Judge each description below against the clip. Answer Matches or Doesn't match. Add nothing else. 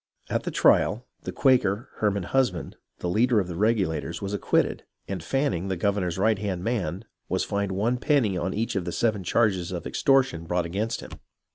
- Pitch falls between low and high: Doesn't match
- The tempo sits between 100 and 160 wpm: Doesn't match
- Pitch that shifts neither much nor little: Matches